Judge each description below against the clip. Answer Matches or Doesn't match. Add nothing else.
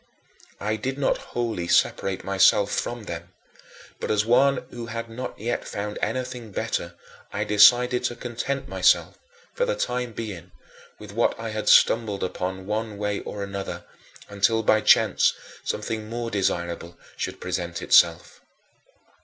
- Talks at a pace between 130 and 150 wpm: Matches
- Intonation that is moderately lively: Matches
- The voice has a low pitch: Matches